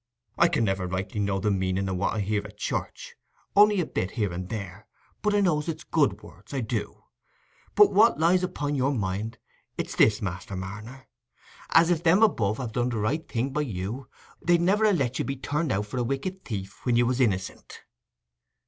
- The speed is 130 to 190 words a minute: No, average, 200 wpm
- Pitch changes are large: Yes, wide, 8.1 semitones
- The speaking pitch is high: No, low, 120 Hz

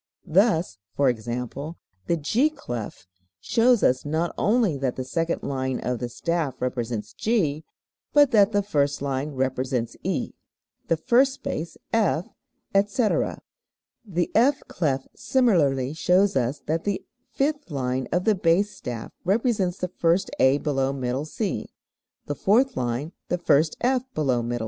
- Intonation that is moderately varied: No, wide, 7.7 semitones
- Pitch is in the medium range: Yes, medium, 160 Hz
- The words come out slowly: No, average, 150 wpm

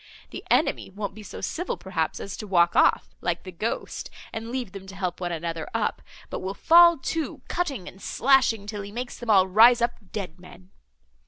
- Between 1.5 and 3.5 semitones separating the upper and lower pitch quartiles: No, average, 4.6 semitones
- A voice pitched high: Yes, high, 200 Hz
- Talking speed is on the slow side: No, average, 200 wpm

